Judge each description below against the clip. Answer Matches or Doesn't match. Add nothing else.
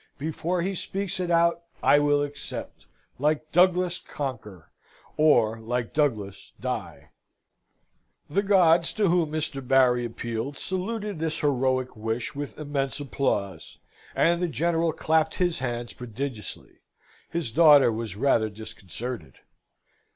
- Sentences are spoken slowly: Matches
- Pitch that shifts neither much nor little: Doesn't match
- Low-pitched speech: Doesn't match